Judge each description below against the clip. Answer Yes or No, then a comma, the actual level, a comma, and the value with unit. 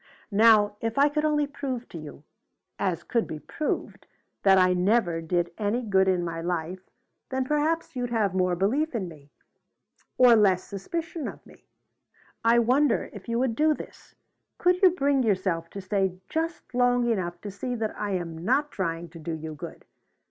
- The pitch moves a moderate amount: No, wide, 6.2 semitones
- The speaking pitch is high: Yes, high, 210 Hz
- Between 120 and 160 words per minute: No, average, 180 wpm